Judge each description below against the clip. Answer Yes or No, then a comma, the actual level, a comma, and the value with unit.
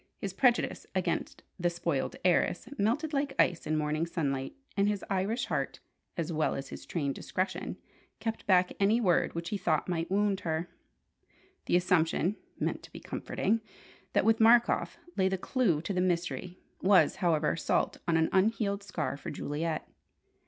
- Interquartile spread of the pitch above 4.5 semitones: No, average, 3.8 semitones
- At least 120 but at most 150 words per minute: No, average, 165 wpm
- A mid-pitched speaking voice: Yes, medium, 180 Hz